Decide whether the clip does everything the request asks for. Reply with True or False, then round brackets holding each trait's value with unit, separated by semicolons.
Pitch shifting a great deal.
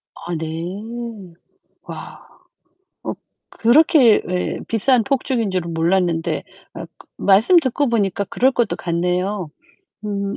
False (5.0 semitones)